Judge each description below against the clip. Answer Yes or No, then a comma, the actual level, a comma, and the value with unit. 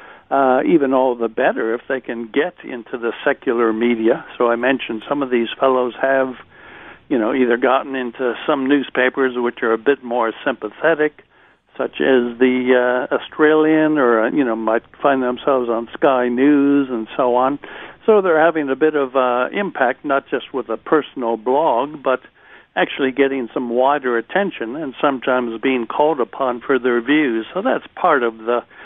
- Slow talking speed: No, average, 175 wpm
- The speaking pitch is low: Yes, low, 130 Hz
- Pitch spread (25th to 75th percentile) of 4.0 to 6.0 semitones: No, average, 2.7 semitones